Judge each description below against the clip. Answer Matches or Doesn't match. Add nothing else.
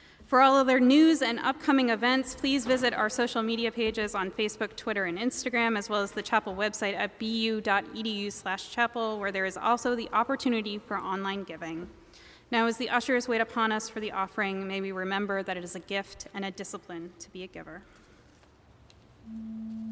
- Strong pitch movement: Doesn't match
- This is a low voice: Doesn't match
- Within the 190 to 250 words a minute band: Doesn't match